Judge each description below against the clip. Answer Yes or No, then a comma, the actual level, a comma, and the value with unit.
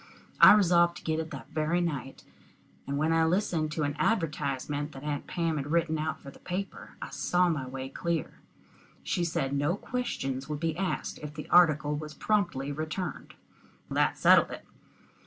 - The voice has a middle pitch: Yes, medium, 155 Hz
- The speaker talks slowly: No, average, 175 wpm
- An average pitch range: Yes, average, 3.0 semitones